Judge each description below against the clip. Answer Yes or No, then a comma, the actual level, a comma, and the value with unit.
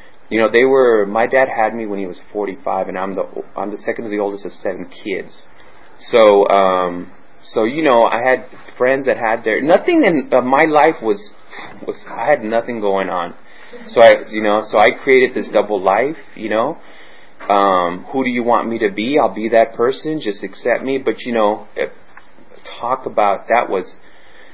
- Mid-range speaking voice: No, low, 115 Hz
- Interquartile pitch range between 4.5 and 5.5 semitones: Yes, average, 4.8 semitones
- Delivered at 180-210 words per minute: Yes, average, 200 wpm